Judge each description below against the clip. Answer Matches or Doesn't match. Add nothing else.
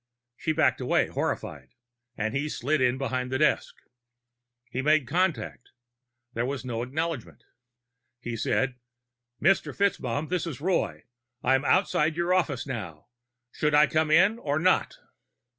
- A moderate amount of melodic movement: Matches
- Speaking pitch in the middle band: Matches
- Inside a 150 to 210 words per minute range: Doesn't match